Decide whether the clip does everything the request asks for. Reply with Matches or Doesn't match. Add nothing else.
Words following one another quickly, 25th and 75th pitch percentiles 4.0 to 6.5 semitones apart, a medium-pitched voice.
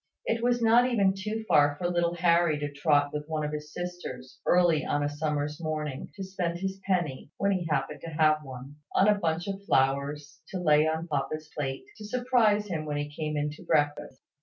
Matches